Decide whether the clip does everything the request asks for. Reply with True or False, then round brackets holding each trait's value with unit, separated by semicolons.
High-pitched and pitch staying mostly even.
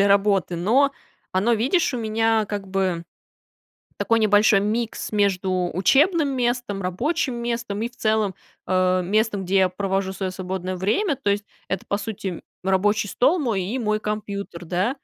False (205 Hz; 3.5 semitones)